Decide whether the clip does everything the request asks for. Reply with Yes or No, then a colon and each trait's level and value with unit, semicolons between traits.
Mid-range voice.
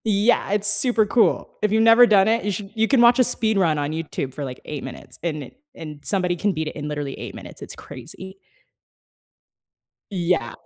No: high, 195 Hz